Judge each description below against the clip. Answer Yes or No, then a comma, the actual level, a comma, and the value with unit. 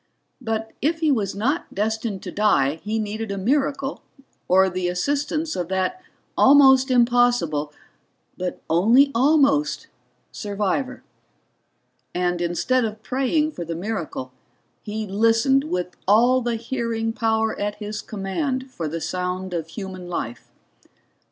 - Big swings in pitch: Yes, wide, 5.7 semitones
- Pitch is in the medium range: No, high, 220 Hz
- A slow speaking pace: Yes, slow, 130 wpm